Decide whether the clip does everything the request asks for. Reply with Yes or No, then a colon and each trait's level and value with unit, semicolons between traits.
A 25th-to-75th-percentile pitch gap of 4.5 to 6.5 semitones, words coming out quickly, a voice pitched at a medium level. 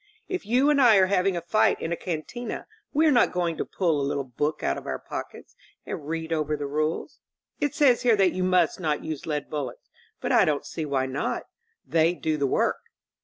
Yes: average, 5.0 semitones; fast, 220 wpm; medium, 165 Hz